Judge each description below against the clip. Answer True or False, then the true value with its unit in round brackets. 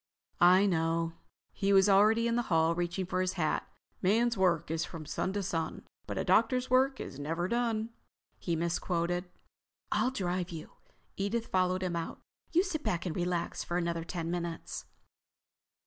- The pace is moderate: True (165 wpm)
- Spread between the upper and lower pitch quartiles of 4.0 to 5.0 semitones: False (3.6 semitones)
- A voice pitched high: False (180 Hz)